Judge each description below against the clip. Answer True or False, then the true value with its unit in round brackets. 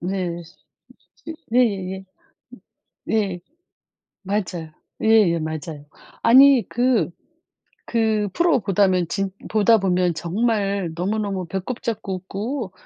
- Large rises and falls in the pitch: False (3.7 semitones)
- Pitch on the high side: True (195 Hz)